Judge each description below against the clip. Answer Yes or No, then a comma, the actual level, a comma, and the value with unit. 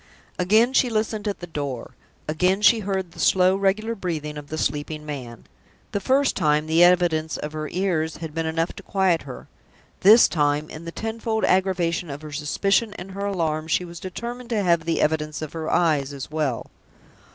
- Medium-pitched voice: Yes, medium, 170 Hz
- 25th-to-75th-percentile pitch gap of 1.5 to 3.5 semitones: No, average, 4.3 semitones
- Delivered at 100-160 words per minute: No, average, 190 wpm